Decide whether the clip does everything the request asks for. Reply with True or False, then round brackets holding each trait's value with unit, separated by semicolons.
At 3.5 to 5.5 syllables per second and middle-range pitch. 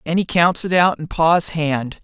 True (4.2 syllables/s; 165 Hz)